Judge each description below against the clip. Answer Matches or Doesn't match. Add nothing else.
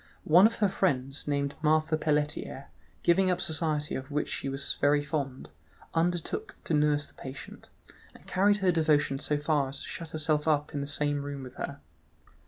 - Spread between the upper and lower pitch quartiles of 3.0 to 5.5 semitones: Doesn't match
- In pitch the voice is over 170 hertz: Doesn't match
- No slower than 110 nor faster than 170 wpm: Doesn't match